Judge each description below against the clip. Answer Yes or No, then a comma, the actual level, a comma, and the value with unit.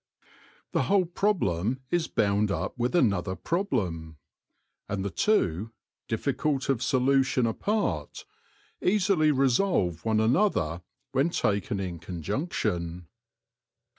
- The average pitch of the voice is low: Yes, low, 115 Hz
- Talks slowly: Yes, slow, 105 wpm